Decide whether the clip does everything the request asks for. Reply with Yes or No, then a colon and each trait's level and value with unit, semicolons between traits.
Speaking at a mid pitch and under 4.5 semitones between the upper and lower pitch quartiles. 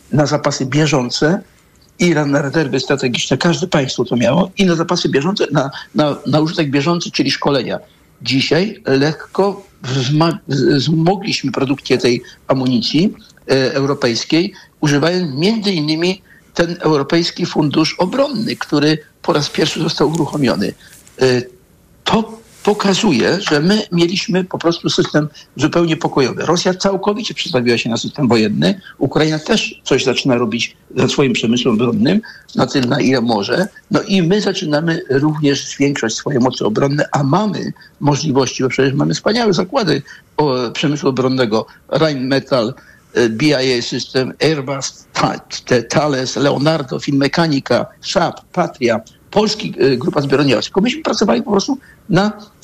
No: medium, 155 Hz; average, 5.1 semitones